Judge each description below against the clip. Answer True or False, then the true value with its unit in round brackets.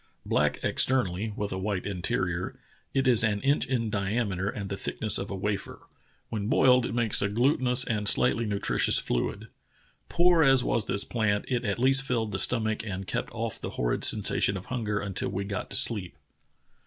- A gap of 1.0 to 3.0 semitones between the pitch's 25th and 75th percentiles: False (3.7 semitones)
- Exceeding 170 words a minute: True (185 wpm)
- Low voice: True (110 Hz)